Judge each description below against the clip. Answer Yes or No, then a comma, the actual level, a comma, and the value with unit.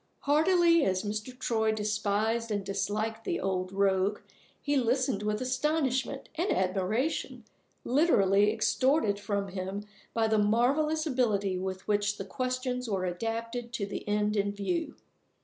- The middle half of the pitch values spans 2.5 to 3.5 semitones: No, average, 4.1 semitones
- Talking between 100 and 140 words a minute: Yes, slow, 135 wpm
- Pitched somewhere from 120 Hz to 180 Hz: No, high, 220 Hz